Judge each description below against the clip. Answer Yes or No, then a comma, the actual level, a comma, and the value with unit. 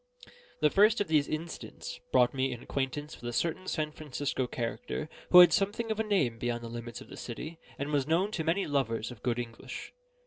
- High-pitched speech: No, medium, 145 Hz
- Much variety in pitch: Yes, wide, 5.9 semitones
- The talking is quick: Yes, fast, 210 wpm